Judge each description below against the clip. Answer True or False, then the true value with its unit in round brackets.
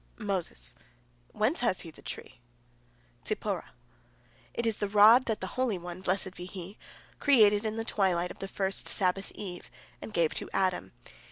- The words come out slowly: False (165 wpm)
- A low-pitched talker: False (195 Hz)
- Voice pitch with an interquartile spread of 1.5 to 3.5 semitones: True (3.2 semitones)